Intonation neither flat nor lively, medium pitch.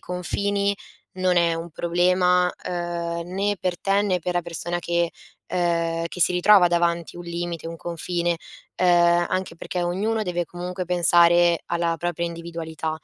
No: narrow, 1.0 semitones; medium, 175 Hz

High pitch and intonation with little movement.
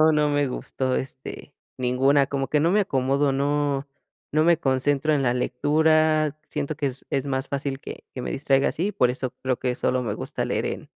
No: medium, 140 Hz; narrow, 2.2 semitones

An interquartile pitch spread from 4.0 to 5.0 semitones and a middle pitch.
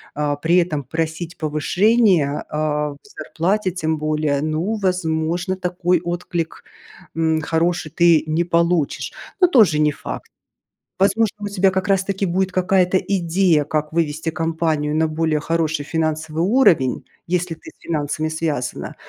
No: average, 2.8 semitones; medium, 165 Hz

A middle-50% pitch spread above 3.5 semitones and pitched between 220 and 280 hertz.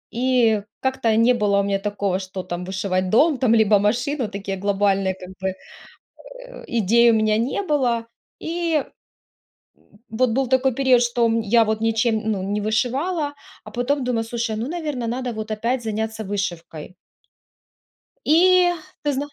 Yes: average, 4.1 semitones; high, 230 Hz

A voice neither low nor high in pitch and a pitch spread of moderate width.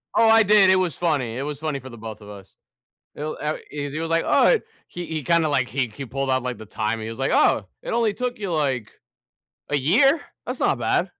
No: medium, 145 Hz; wide, 5.9 semitones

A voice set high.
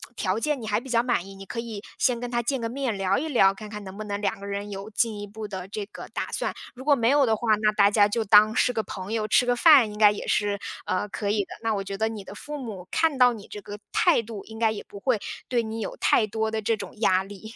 Yes: high, 215 Hz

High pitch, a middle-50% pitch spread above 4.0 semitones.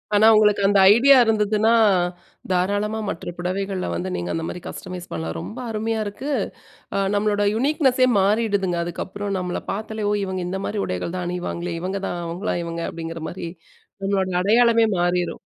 No: high, 195 Hz; average, 3.4 semitones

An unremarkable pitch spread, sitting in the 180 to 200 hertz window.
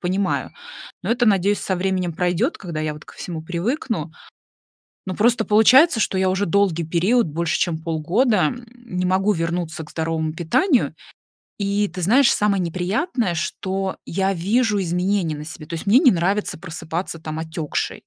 Yes: average, 3.9 semitones; medium, 185 Hz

